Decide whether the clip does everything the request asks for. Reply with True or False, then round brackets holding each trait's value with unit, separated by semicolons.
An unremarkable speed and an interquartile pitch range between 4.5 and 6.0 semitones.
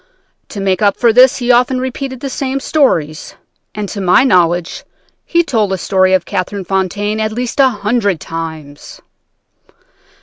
True (160 wpm; 5.2 semitones)